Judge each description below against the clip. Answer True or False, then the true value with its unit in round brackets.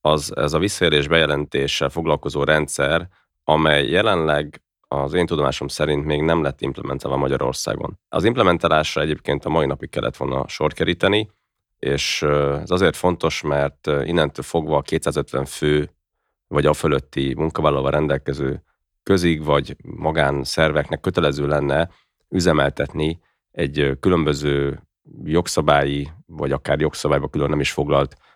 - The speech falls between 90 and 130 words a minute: True (125 wpm)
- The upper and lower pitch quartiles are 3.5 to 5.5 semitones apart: False (2.6 semitones)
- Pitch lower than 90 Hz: True (75 Hz)